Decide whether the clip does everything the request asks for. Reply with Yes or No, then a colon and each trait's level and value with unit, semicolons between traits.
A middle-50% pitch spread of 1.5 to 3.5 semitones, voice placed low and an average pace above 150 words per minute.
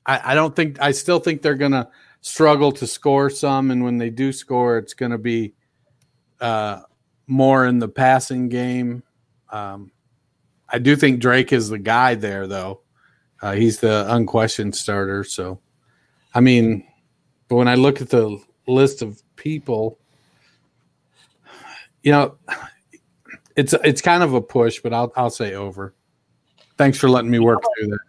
Yes: average, 3.2 semitones; low, 125 Hz; average, 160 wpm